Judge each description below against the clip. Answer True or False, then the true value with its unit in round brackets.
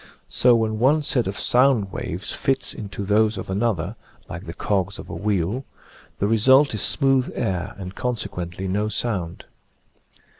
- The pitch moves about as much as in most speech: True (4.2 semitones)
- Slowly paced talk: False (155 wpm)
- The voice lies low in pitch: True (105 Hz)